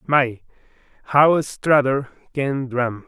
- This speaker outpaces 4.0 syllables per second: No, 3.0 syllables/s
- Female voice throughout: No, male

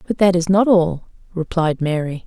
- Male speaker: No, female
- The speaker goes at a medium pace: Yes, average, 185 wpm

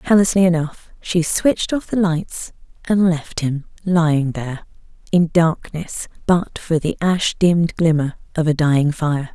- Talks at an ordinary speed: Yes, average, 155 wpm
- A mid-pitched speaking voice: Yes, medium, 165 Hz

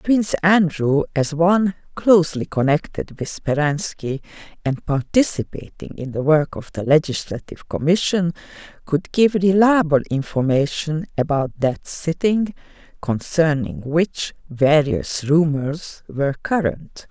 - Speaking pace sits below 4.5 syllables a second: Yes, 4.2 syllables/s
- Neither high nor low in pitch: Yes, medium, 160 Hz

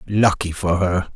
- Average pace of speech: Yes, average, 155 wpm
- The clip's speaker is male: Yes, male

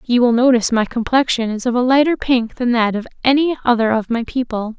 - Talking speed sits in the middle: No, fast, 225 wpm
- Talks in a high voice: Yes, high, 240 Hz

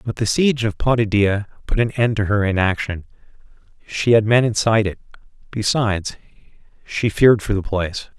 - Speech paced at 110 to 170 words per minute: Yes, average, 160 wpm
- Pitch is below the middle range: Yes, low, 110 Hz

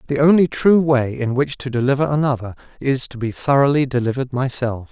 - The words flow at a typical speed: Yes, average, 185 wpm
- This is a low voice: Yes, low, 130 Hz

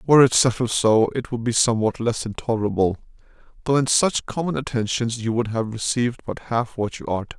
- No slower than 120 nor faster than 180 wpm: No, average, 195 wpm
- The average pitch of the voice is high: No, low, 120 Hz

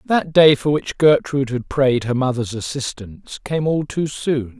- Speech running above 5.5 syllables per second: No, 4.5 syllables/s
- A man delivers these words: Yes, male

